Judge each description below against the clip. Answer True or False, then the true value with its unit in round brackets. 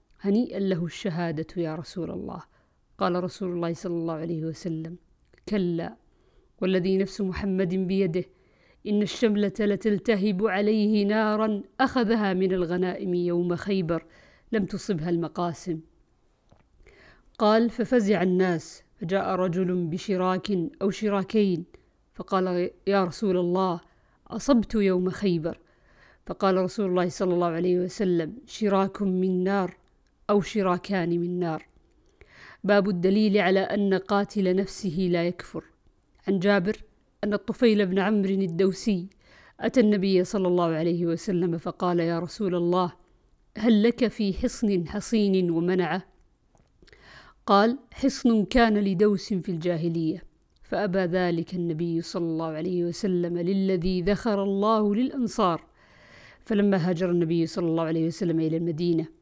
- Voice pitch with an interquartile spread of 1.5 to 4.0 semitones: True (2.8 semitones)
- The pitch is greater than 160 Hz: True (185 Hz)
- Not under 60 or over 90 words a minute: False (120 wpm)